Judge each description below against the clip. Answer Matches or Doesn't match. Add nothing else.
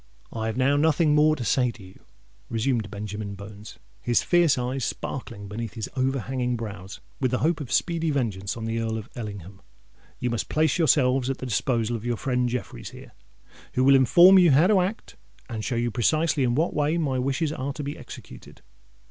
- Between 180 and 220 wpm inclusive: Matches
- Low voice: Matches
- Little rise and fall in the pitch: Doesn't match